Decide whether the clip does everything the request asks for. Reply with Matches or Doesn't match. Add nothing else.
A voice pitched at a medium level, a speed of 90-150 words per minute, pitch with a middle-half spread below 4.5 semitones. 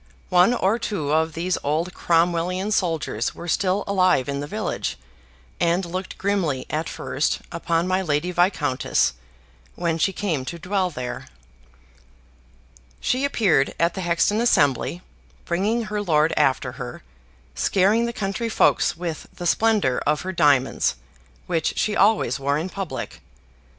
Matches